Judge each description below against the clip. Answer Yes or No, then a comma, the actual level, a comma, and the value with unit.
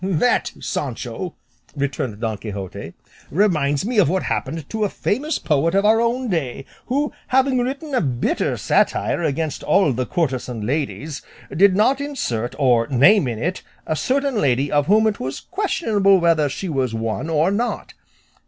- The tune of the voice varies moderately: No, wide, 8.3 semitones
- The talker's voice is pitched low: No, medium, 165 Hz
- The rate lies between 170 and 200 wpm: No, average, 160 wpm